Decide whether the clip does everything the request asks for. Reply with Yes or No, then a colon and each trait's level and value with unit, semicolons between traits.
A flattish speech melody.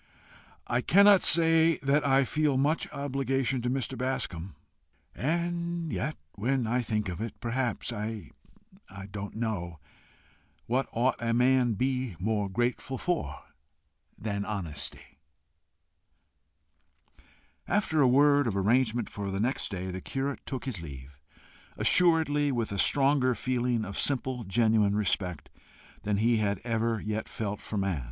No: average, 4.7 semitones